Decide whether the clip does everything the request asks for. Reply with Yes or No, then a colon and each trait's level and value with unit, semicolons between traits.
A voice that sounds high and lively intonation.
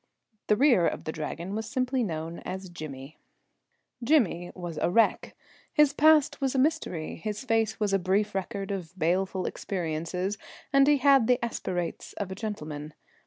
Yes: high, 195 Hz; wide, 6.3 semitones